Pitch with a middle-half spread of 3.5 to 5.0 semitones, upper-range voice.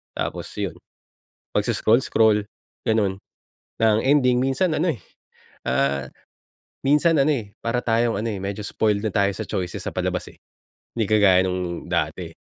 No: average, 4.5 semitones; low, 110 Hz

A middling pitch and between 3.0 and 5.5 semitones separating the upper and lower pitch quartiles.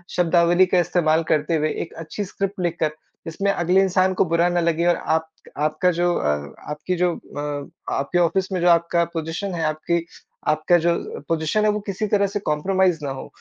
No: medium, 170 Hz; narrow, 2.6 semitones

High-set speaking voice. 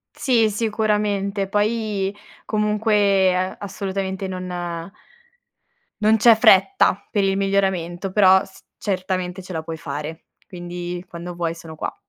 Yes: high, 195 Hz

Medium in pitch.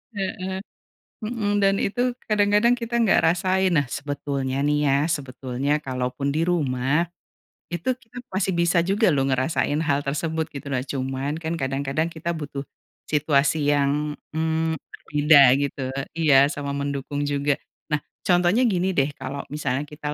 Yes: medium, 150 Hz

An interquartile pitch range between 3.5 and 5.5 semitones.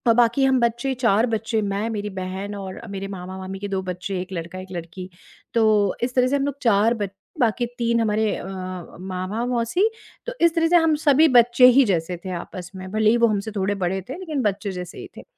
Yes: average, 4.3 semitones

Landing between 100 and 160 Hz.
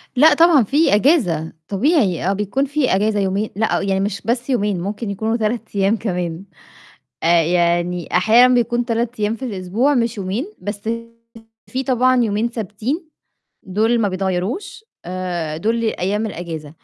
No: high, 210 Hz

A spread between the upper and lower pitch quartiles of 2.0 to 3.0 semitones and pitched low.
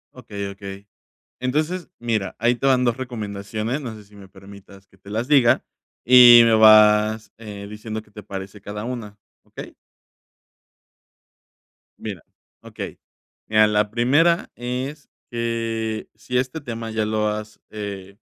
Yes: average, 2.7 semitones; low, 110 Hz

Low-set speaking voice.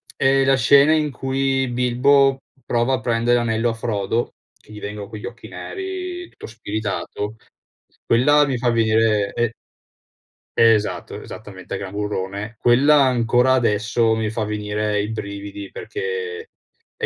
Yes: low, 115 Hz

